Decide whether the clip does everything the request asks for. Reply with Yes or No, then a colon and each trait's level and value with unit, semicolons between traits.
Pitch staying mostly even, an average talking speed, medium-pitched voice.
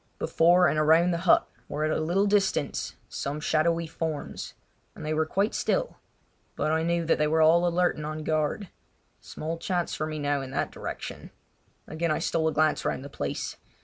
Yes: narrow, 1.9 semitones; average, 190 wpm; medium, 160 Hz